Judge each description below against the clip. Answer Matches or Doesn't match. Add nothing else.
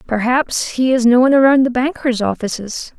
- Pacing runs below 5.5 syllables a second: Matches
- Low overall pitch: Doesn't match